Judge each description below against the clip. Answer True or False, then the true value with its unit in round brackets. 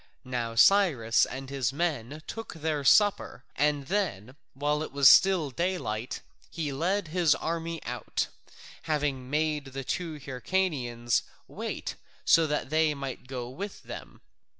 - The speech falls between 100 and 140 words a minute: True (135 wpm)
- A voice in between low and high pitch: True (150 Hz)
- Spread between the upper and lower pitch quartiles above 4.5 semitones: False (4.1 semitones)